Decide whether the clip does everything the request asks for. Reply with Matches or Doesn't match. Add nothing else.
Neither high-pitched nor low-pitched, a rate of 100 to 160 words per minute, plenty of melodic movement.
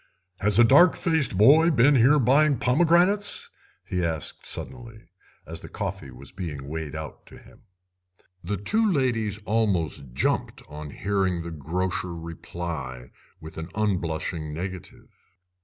Doesn't match